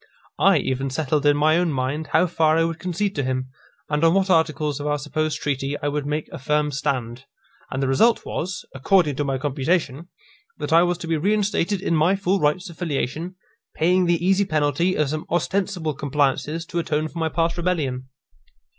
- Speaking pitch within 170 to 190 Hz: No, medium, 155 Hz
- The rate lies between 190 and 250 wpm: Yes, average, 200 wpm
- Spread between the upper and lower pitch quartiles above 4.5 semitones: No, average, 3.3 semitones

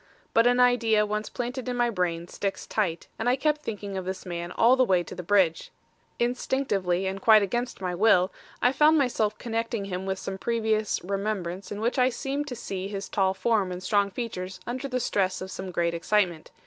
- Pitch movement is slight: No, average, 4.3 semitones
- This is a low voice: No, high, 205 Hz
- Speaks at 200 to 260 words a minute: Yes, fast, 205 wpm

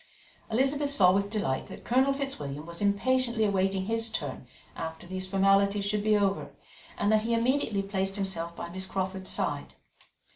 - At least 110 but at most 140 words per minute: No, average, 160 wpm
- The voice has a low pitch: No, high, 200 Hz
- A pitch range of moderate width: Yes, average, 3.2 semitones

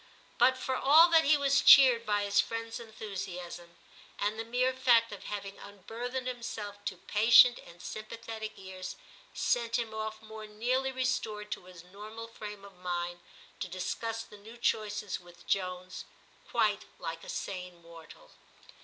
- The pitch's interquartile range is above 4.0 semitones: No, average, 3.7 semitones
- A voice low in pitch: No, high, 215 Hz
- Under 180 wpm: Yes, average, 155 wpm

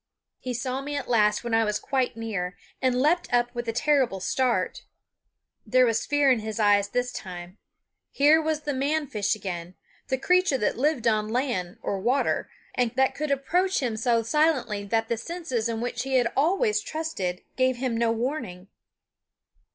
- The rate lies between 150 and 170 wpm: No, average, 180 wpm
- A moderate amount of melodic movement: Yes, average, 4.4 semitones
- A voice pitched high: Yes, high, 245 Hz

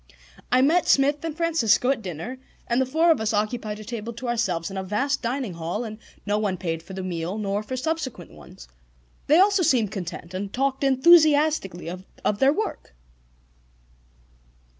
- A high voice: Yes, high, 230 Hz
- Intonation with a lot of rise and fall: Yes, wide, 6.2 semitones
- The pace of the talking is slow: No, average, 175 wpm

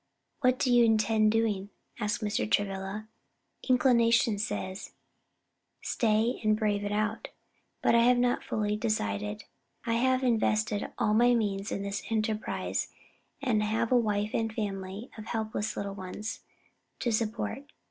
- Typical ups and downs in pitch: No, narrow, 2.2 semitones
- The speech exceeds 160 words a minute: No, average, 145 wpm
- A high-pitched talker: Yes, high, 215 Hz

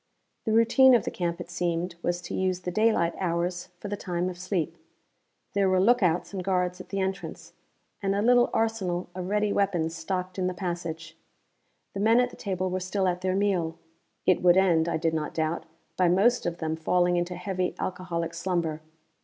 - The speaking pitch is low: No, medium, 180 Hz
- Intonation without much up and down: Yes, narrow, 2.2 semitones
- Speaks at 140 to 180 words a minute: No, average, 195 wpm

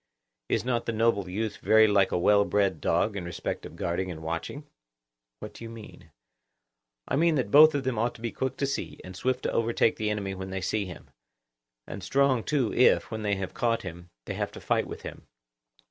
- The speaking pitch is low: Yes, low, 110 Hz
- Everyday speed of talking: No, fast, 220 wpm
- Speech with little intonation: No, average, 4.2 semitones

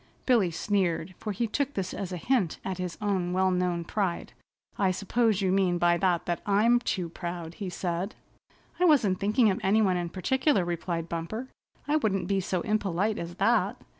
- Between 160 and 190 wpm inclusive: Yes, average, 185 wpm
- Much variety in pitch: No, average, 3.3 semitones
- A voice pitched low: No, high, 190 Hz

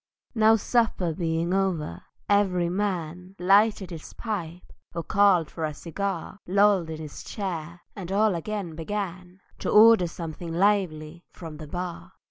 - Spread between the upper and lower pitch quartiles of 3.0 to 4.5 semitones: Yes, average, 3.5 semitones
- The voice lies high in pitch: No, medium, 180 Hz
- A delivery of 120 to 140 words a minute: Yes, slow, 135 wpm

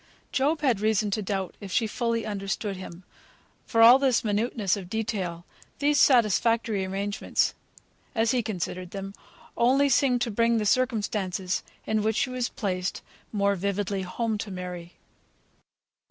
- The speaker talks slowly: No, average, 145 wpm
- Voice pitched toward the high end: Yes, high, 210 Hz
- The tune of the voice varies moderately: Yes, average, 3.4 semitones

